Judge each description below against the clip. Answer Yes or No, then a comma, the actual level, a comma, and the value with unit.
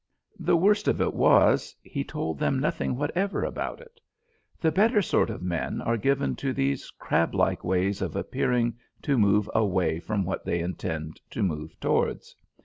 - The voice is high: No, low, 110 Hz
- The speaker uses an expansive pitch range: Yes, wide, 8.3 semitones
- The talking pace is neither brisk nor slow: Yes, average, 165 wpm